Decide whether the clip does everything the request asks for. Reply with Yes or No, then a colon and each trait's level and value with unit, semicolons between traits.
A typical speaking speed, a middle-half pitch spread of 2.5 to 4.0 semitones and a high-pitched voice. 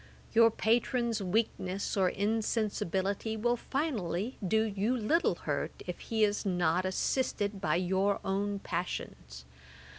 No: slow, 120 wpm; average, 3.2 semitones; high, 205 Hz